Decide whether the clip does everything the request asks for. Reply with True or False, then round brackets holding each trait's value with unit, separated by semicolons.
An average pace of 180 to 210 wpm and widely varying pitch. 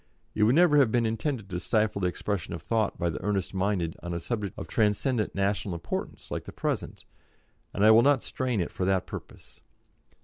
False (205 wpm; 3.8 semitones)